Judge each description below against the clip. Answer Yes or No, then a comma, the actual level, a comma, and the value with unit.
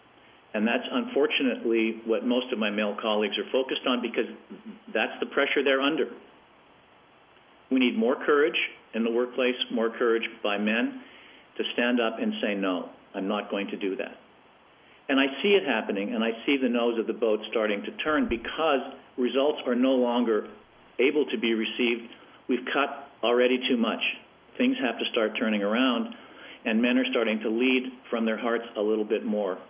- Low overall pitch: Yes, low, 125 Hz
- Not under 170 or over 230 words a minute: Yes, average, 180 wpm